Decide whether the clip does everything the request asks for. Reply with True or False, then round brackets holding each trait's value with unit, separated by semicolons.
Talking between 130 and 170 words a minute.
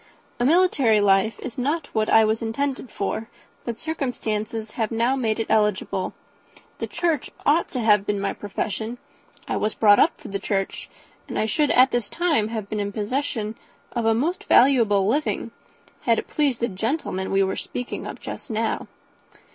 False (180 wpm)